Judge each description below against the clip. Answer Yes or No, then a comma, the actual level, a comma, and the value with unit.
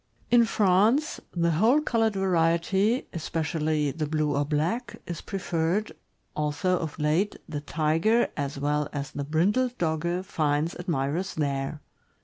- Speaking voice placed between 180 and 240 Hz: No, medium, 165 Hz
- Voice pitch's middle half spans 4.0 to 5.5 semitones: Yes, average, 4.5 semitones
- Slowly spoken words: Yes, slow, 130 wpm